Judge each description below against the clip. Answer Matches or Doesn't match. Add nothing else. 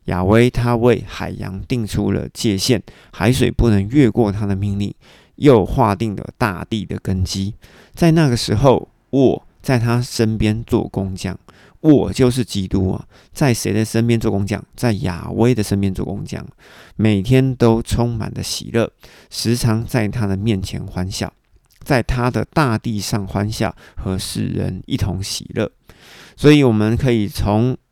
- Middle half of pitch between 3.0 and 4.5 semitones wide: Matches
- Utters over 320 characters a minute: Doesn't match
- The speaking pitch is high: Doesn't match